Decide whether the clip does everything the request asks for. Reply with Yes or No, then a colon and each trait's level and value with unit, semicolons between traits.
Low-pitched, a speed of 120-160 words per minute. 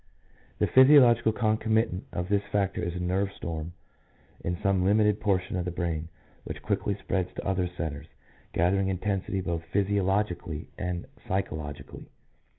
Yes: very low, 95 Hz; average, 140 wpm